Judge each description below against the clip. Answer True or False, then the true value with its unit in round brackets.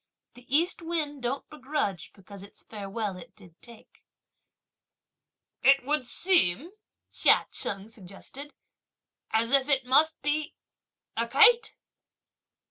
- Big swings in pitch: True (6.5 semitones)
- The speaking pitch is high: True (260 Hz)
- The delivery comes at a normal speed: False (115 wpm)